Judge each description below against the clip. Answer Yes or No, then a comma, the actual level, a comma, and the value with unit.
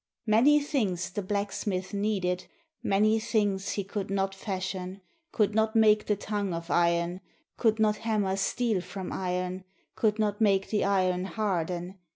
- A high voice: Yes, high, 200 Hz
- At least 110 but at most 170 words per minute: Yes, average, 150 wpm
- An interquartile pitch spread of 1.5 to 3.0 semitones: Yes, narrow, 2.6 semitones